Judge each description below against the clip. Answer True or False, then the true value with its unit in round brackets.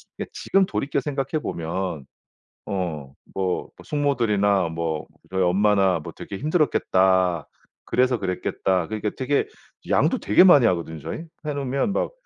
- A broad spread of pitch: True (7.2 semitones)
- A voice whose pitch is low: True (100 Hz)